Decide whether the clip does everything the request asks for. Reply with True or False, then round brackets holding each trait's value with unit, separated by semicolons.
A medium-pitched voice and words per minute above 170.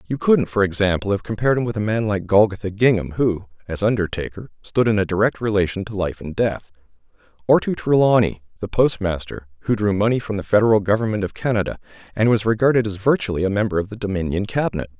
False (105 Hz; 200 wpm)